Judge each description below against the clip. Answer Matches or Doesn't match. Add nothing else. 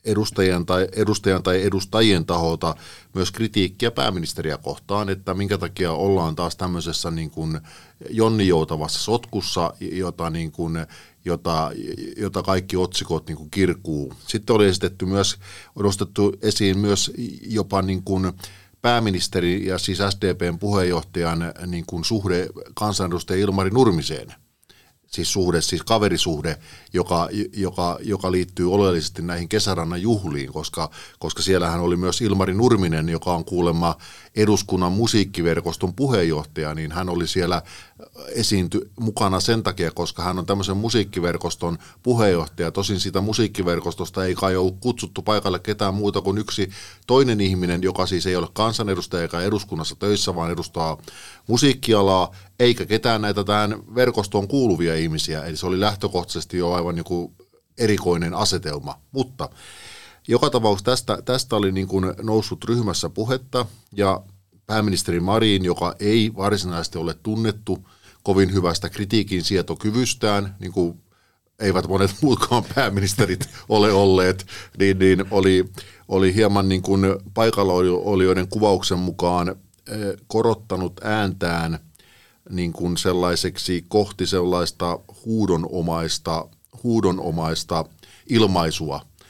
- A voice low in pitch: Matches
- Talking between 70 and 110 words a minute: Doesn't match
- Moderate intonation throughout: Matches